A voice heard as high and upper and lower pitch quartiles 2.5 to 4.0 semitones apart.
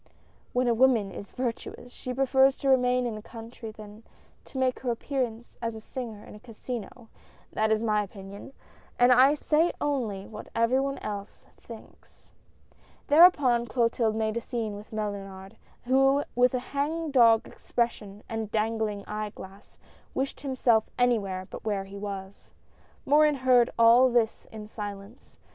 Yes: high, 230 Hz; average, 3.3 semitones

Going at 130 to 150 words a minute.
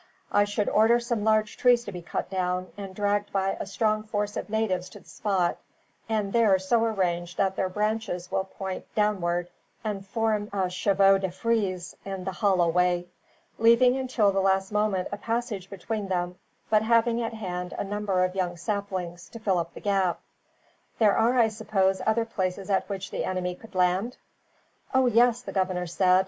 No: average, 185 wpm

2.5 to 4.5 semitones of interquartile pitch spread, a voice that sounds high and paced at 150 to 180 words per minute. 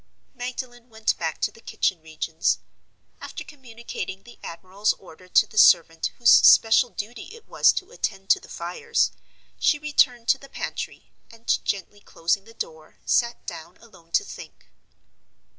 No: average, 5.3 semitones; high, 225 Hz; average, 155 wpm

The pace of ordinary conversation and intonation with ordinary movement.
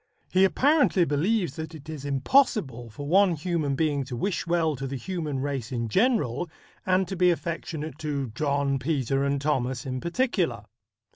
Yes: average, 165 wpm; average, 4.8 semitones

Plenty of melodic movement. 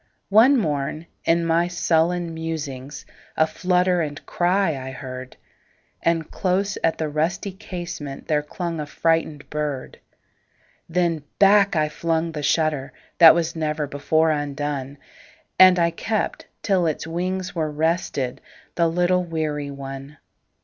No: average, 3.1 semitones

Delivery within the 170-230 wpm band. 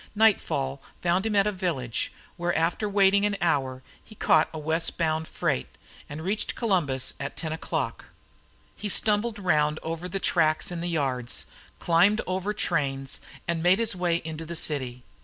No: average, 160 wpm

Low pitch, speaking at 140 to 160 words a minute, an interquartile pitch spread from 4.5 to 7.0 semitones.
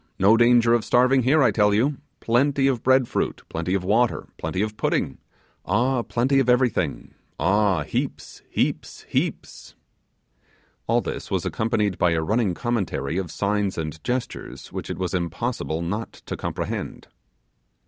Yes: low, 110 Hz; average, 150 wpm; average, 5.0 semitones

